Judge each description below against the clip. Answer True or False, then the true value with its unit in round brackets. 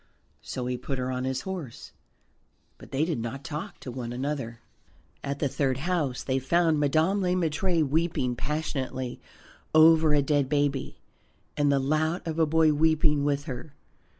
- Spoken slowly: False (165 wpm)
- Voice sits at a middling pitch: True (145 Hz)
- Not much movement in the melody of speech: False (3.3 semitones)